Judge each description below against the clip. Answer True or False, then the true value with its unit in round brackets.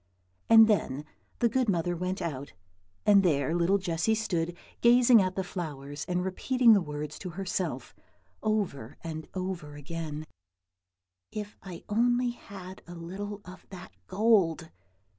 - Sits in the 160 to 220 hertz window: True (185 Hz)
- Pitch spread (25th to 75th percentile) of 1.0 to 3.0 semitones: False (4.2 semitones)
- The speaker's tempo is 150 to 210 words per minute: False (140 wpm)